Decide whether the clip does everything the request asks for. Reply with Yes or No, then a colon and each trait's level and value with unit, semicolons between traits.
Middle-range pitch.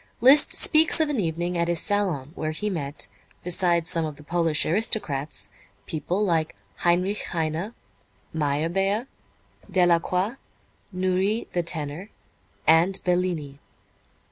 Yes: medium, 175 Hz